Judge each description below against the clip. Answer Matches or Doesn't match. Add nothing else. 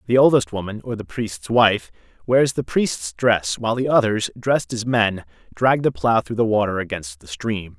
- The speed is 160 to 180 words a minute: Doesn't match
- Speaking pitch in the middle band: Doesn't match